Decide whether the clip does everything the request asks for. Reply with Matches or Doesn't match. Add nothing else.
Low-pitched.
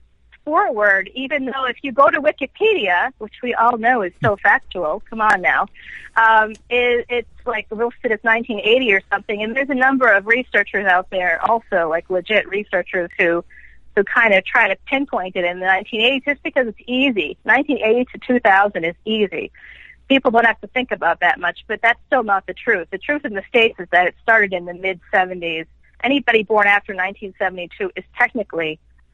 Doesn't match